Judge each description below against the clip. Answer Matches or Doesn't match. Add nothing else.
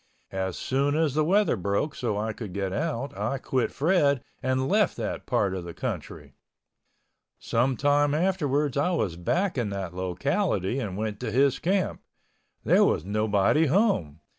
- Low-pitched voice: Matches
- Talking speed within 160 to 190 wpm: Matches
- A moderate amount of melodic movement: Doesn't match